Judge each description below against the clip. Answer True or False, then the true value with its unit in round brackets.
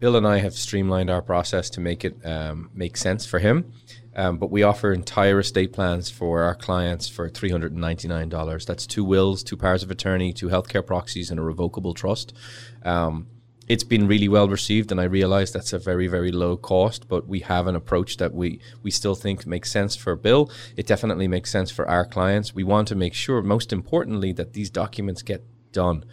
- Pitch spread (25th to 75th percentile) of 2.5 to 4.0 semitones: True (3.1 semitones)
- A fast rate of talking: True (215 wpm)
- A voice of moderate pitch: False (95 Hz)